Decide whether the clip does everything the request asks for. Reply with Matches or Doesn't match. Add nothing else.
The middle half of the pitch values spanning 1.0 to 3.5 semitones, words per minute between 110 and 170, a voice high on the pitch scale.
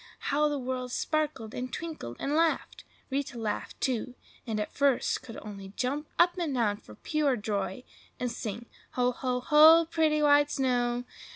Doesn't match